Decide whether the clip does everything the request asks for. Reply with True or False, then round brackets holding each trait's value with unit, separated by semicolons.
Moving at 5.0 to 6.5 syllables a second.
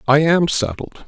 False (4.4 syllables/s)